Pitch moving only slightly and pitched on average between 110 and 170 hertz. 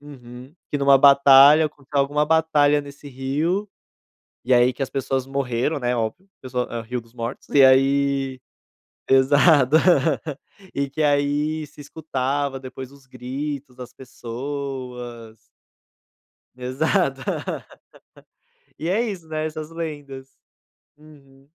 Yes: narrow, 2.3 semitones; medium, 140 Hz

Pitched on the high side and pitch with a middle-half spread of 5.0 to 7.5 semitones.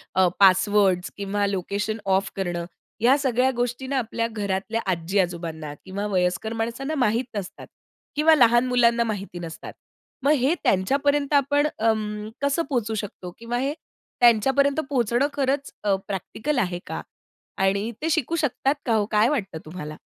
Yes: high, 225 Hz; wide, 5.6 semitones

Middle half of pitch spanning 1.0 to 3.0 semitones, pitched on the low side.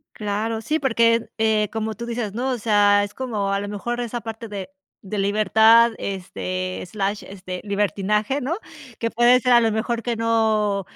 No: narrow, 2.4 semitones; high, 220 Hz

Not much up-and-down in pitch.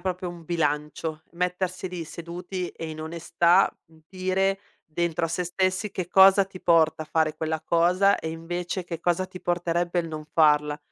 Yes: narrow, 2.3 semitones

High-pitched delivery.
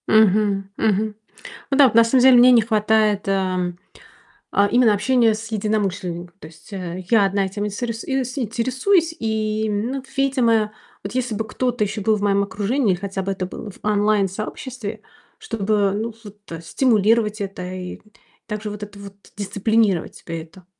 Yes: high, 210 Hz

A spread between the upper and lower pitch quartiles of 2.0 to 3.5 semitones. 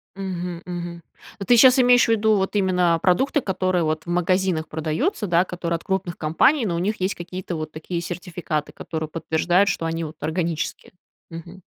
Yes: narrow, 2.6 semitones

